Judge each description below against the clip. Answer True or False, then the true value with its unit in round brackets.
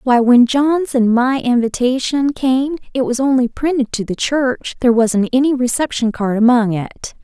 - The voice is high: True (250 Hz)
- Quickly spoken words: False (165 wpm)